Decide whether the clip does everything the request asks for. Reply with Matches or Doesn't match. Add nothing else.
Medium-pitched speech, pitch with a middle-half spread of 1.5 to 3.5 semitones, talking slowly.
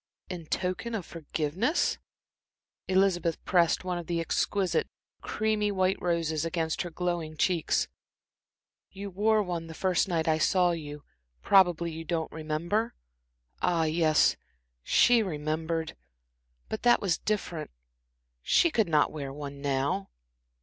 Matches